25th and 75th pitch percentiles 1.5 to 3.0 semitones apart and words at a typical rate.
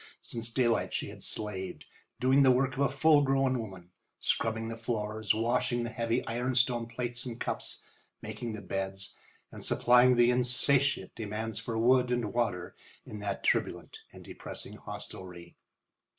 Yes: narrow, 2.6 semitones; average, 150 wpm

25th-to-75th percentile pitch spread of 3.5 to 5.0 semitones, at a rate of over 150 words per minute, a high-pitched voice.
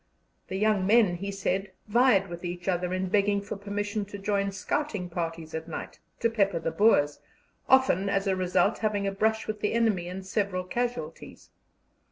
No: narrow, 2.5 semitones; average, 180 wpm; high, 195 Hz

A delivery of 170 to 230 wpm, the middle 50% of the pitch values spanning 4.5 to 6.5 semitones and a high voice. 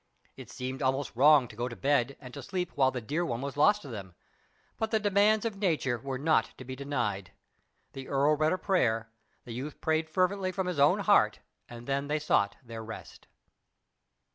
No: average, 200 wpm; average, 4.9 semitones; medium, 140 Hz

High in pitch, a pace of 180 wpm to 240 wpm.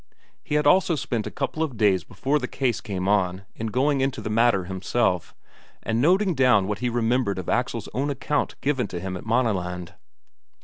No: low, 120 Hz; average, 185 wpm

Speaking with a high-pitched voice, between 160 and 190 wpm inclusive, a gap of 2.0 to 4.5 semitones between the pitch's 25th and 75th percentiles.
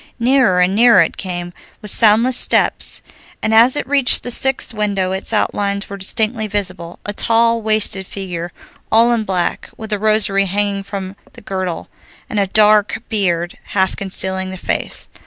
Yes: high, 205 Hz; average, 165 wpm; average, 2.8 semitones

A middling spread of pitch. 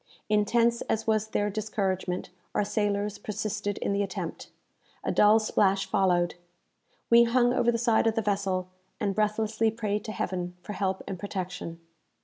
No: narrow, 2.2 semitones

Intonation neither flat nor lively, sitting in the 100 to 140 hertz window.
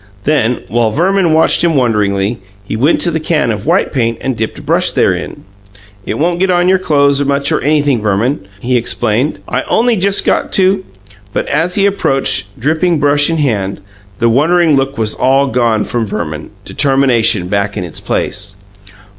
No: wide, 6.5 semitones; low, 135 Hz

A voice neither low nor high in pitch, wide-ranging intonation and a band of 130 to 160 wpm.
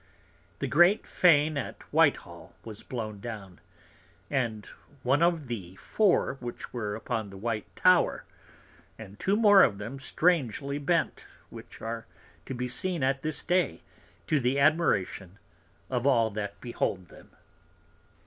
No: low, 125 Hz; wide, 6.3 semitones; average, 140 wpm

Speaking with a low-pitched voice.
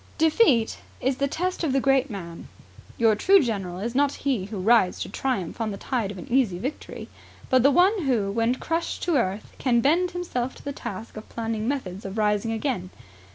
No: high, 240 Hz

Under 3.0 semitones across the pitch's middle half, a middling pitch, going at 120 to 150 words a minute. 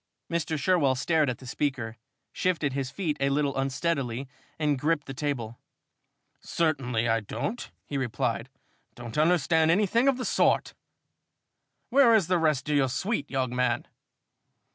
No: average, 4.4 semitones; medium, 145 Hz; average, 145 wpm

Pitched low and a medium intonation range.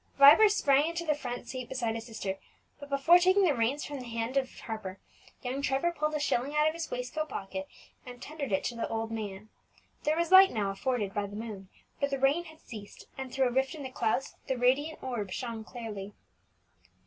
No: very high, 255 Hz; average, 4.7 semitones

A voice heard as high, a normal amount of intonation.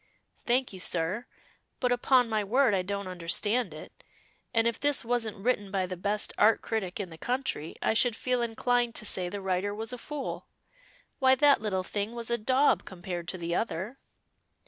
Yes: high, 215 Hz; average, 4.5 semitones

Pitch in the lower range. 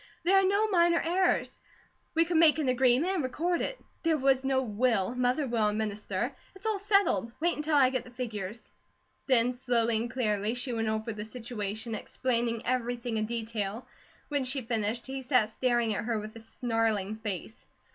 No: high, 245 Hz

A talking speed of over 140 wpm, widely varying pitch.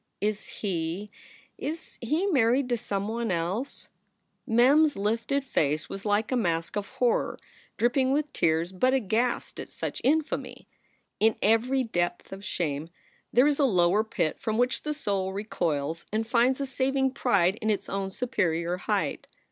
Yes: average, 160 wpm; wide, 5.7 semitones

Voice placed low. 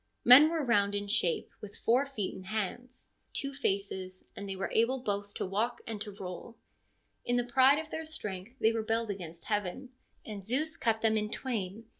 No: high, 220 Hz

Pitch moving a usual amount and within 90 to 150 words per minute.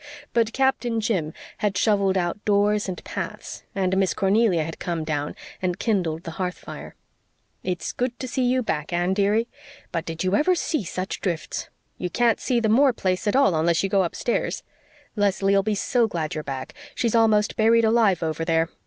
No: average, 4.6 semitones; average, 190 wpm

